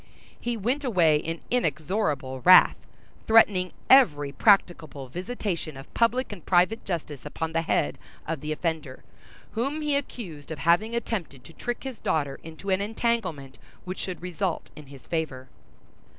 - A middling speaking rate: Yes, average, 150 wpm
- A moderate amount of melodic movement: No, wide, 6.7 semitones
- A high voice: No, medium, 175 Hz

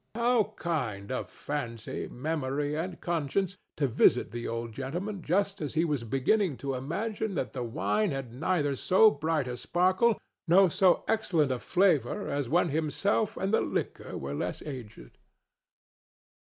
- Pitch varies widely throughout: Yes, wide, 6.5 semitones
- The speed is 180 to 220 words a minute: No, average, 155 wpm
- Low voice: No, medium, 155 Hz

